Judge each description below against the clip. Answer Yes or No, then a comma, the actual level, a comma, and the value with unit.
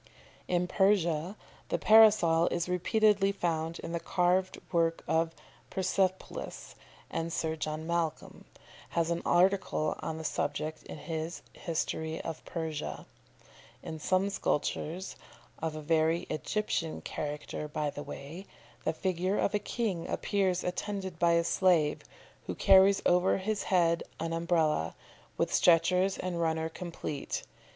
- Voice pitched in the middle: Yes, medium, 170 Hz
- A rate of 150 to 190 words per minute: No, slow, 135 wpm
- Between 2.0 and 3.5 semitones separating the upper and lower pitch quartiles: Yes, average, 2.7 semitones